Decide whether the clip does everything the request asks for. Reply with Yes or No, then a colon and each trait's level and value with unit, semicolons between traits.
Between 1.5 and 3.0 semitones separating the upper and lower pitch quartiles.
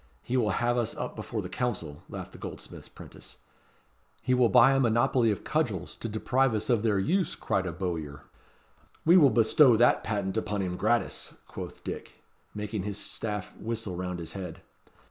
No: average, 4.3 semitones